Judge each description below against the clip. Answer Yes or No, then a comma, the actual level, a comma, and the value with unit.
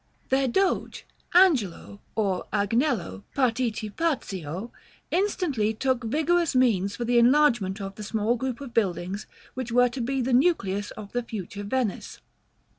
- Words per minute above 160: No, slow, 135 wpm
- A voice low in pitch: No, high, 235 Hz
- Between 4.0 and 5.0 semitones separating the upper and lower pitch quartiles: Yes, average, 4.5 semitones